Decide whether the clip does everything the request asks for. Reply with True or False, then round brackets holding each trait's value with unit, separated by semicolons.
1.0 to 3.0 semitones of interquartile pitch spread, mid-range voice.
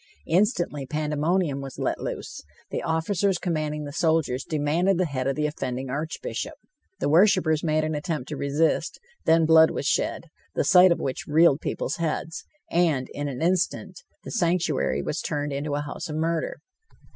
True (2.7 semitones; 155 Hz)